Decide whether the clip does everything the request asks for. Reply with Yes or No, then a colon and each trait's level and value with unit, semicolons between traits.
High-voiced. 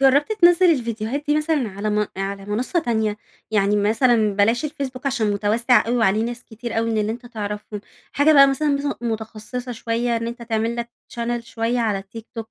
Yes: high, 230 Hz